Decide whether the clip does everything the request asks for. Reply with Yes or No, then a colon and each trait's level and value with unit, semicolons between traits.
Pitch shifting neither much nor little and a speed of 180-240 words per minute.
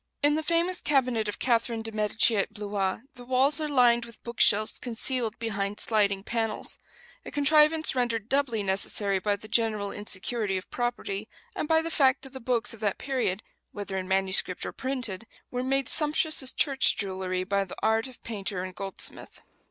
Yes: average, 4.6 semitones; average, 185 wpm